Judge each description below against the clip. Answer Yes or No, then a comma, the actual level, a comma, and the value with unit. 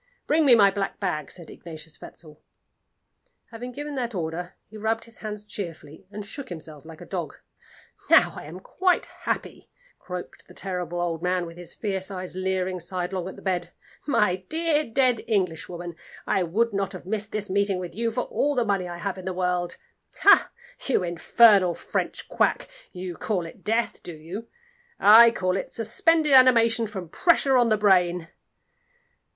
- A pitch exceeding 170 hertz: Yes, high, 190 Hz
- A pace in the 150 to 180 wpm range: Yes, average, 175 wpm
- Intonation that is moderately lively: Yes, average, 4.4 semitones